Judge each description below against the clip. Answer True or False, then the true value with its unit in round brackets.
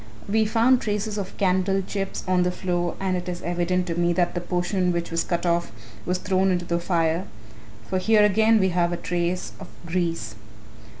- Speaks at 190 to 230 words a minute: True (195 wpm)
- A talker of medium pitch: True (180 Hz)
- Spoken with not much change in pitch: True (1.9 semitones)